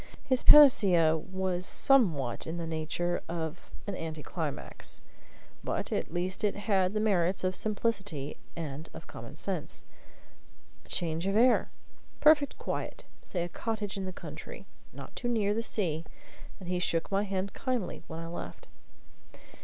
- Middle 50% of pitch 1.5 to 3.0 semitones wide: No, average, 4.1 semitones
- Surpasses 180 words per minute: No, average, 155 wpm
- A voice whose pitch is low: No, medium, 185 Hz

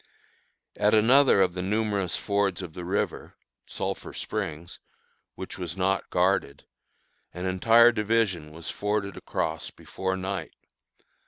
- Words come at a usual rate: No, slow, 120 wpm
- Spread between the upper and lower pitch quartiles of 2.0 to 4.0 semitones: Yes, average, 2.8 semitones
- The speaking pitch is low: Yes, very low, 95 Hz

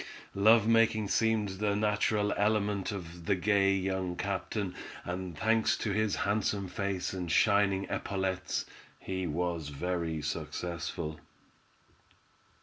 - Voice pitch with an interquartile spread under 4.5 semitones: Yes, average, 2.7 semitones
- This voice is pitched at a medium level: No, very low, 95 Hz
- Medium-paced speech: No, slow, 115 wpm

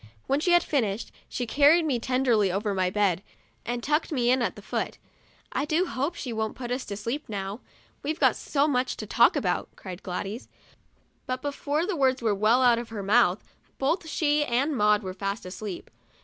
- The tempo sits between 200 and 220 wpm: Yes, fast, 205 wpm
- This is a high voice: Yes, high, 245 Hz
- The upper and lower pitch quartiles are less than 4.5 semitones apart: No, wide, 5.6 semitones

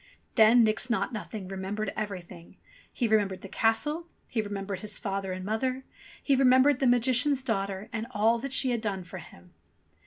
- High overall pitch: Yes, high, 220 Hz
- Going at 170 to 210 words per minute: Yes, average, 175 wpm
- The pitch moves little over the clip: No, average, 4.2 semitones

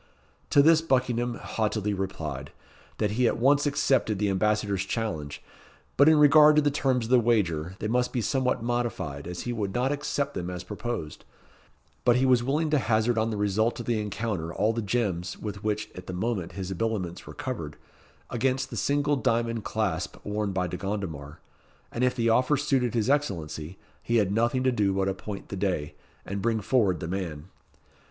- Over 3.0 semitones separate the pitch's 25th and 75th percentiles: Yes, average, 4.6 semitones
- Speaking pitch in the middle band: No, low, 110 Hz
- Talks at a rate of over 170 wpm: Yes, average, 190 wpm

